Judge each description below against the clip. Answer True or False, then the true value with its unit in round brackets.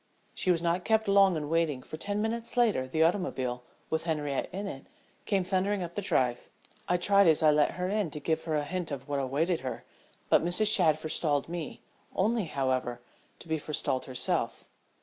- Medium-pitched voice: True (165 Hz)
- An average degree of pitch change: True (4.8 semitones)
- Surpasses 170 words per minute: True (195 wpm)